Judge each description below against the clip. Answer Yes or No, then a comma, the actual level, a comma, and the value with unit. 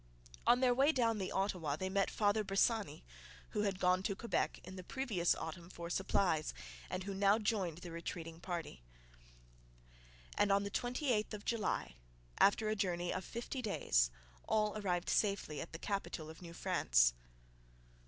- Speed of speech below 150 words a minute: No, average, 165 wpm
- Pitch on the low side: No, high, 195 Hz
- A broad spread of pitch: No, average, 3.7 semitones